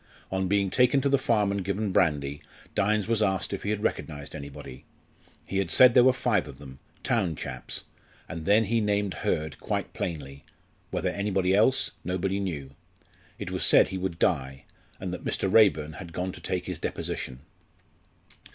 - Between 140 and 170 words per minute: No, average, 180 wpm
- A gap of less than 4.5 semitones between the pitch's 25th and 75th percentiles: No, average, 5.0 semitones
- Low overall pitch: Yes, very low, 95 Hz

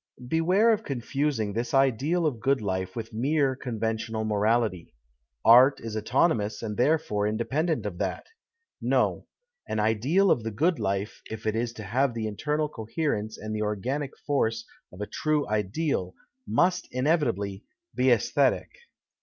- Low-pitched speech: Yes, low, 115 Hz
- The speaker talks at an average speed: Yes, average, 150 wpm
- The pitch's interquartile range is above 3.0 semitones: Yes, wide, 5.4 semitones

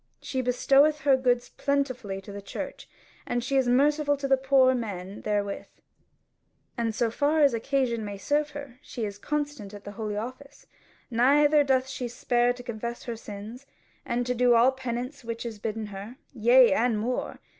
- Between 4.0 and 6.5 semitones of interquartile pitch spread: No, average, 3.6 semitones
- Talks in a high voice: Yes, high, 245 Hz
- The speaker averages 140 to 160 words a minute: No, average, 170 wpm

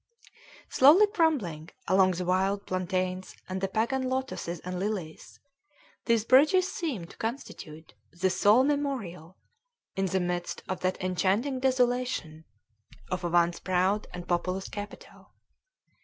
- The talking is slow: Yes, slow, 125 wpm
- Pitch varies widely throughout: Yes, wide, 6.0 semitones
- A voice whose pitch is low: No, high, 190 Hz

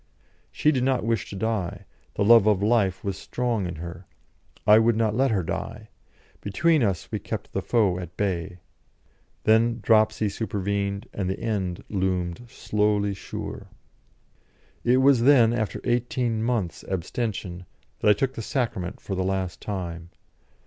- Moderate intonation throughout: Yes, average, 3.7 semitones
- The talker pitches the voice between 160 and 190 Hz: No, low, 105 Hz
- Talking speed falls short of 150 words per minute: No, average, 155 wpm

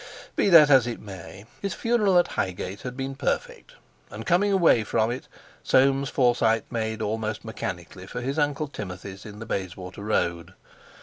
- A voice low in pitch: Yes, low, 115 Hz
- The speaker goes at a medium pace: Yes, average, 165 wpm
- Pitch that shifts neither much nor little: No, wide, 5.7 semitones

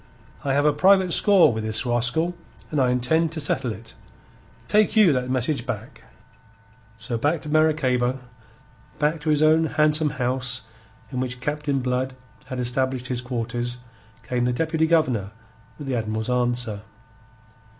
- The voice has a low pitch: Yes, low, 130 Hz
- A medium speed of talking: Yes, average, 150 wpm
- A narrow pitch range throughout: No, average, 4.0 semitones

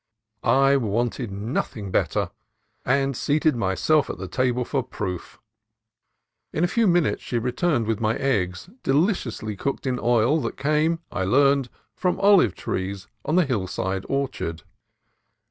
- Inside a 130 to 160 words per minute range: Yes, average, 145 wpm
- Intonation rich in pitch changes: Yes, wide, 5.8 semitones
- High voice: No, low, 125 Hz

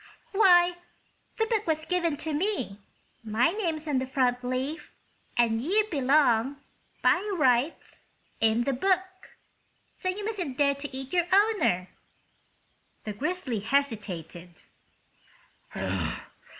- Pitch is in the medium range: No, very high, 285 Hz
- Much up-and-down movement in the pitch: Yes, wide, 6.7 semitones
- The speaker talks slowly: Yes, slow, 115 wpm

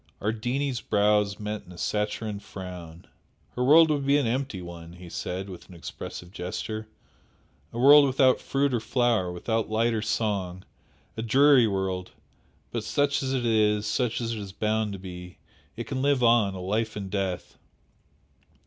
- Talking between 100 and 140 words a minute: No, average, 170 wpm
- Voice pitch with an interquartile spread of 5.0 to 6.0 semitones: No, average, 4.6 semitones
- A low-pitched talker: Yes, low, 110 Hz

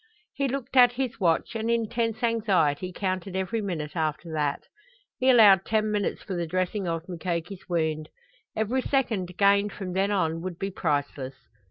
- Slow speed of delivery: No, average, 170 wpm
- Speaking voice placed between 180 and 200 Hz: Yes, high, 190 Hz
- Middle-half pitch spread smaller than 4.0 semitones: No, average, 4.9 semitones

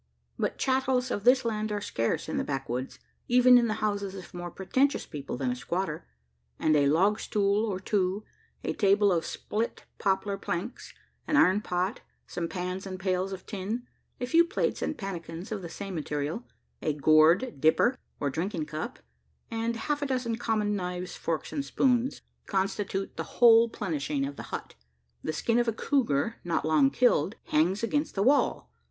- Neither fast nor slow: Yes, average, 175 wpm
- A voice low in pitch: No, high, 195 Hz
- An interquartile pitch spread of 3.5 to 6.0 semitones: Yes, wide, 5.6 semitones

